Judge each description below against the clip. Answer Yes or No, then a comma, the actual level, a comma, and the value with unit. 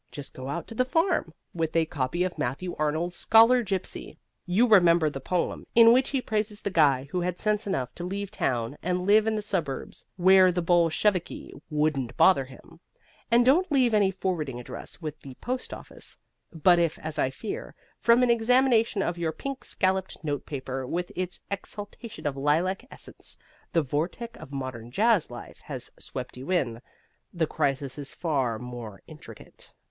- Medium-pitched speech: Yes, medium, 175 Hz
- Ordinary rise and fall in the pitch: No, wide, 6.8 semitones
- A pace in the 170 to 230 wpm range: Yes, average, 175 wpm